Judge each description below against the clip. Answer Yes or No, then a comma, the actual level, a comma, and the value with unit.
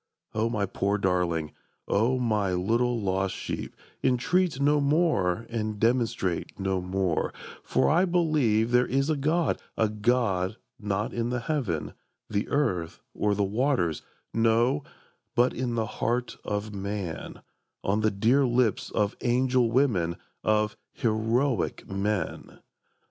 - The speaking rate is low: Yes, slow, 130 wpm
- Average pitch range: Yes, average, 4.2 semitones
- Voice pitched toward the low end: Yes, low, 110 Hz